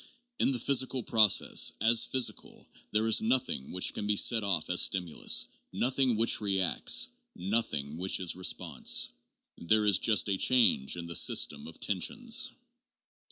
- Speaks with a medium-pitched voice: No, low, 105 Hz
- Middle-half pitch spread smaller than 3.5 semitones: No, average, 4.8 semitones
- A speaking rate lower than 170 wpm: Yes, average, 150 wpm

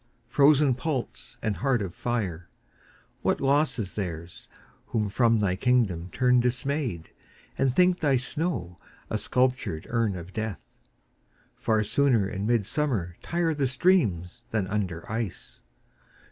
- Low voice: Yes, low, 115 Hz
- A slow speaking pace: Yes, slow, 130 wpm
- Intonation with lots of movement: Yes, wide, 5.9 semitones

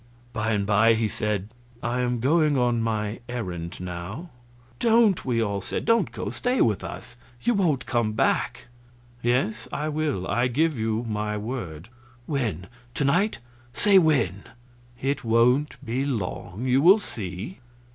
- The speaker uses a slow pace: No, average, 150 wpm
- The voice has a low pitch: Yes, low, 120 Hz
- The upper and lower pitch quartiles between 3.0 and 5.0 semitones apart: No, wide, 5.6 semitones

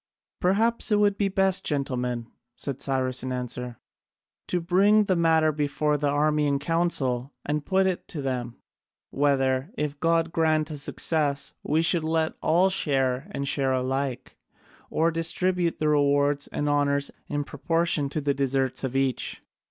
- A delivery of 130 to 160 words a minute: Yes, average, 155 wpm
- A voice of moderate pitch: Yes, medium, 145 Hz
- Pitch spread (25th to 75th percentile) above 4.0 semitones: No, average, 3.5 semitones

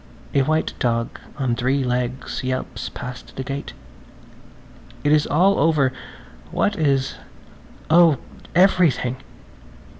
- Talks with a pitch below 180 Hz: Yes, low, 135 Hz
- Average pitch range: Yes, average, 3.7 semitones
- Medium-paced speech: No, slow, 110 wpm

